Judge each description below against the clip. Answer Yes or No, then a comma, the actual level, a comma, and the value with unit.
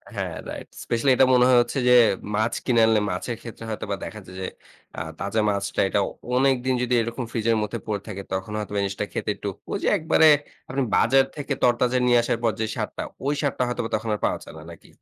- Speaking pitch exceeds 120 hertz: No, low, 115 Hz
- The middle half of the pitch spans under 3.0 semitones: No, average, 3.3 semitones